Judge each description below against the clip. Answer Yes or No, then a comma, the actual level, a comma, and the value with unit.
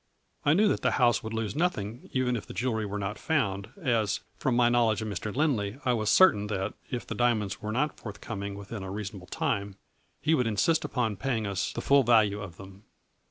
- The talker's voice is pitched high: No, low, 110 Hz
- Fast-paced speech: Yes, fast, 215 wpm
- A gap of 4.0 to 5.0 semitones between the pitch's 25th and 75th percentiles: No, average, 3.5 semitones